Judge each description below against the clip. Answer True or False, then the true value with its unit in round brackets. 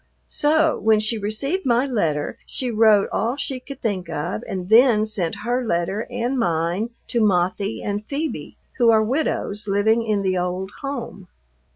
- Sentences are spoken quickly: False (165 wpm)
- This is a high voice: True (215 Hz)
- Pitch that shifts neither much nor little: True (4.3 semitones)